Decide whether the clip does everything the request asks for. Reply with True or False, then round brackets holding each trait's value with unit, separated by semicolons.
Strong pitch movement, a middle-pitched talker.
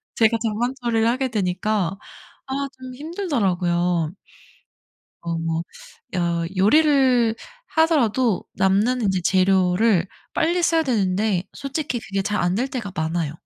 False (6.0 semitones; 210 Hz)